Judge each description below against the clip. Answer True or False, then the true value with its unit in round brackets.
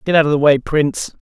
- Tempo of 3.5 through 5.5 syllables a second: False (6.5 syllables/s)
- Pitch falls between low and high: True (150 Hz)